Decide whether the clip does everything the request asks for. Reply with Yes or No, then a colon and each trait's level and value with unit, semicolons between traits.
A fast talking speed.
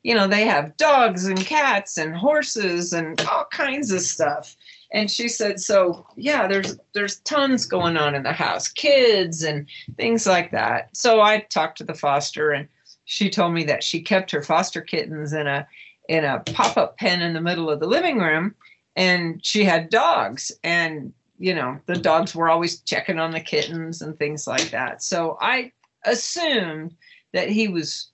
No: average, 185 wpm